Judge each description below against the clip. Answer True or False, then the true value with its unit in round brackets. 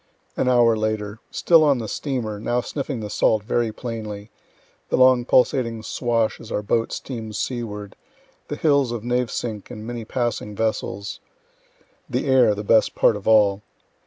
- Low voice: True (115 Hz)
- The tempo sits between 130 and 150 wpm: False (160 wpm)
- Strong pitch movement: False (2.5 semitones)